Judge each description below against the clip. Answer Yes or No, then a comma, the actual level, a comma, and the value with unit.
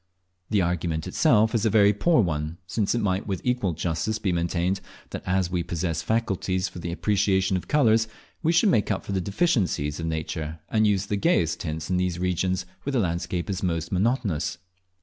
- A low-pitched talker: Yes, very low, 95 Hz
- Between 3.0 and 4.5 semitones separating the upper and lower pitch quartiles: Yes, average, 3.9 semitones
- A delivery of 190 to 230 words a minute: Yes, average, 195 wpm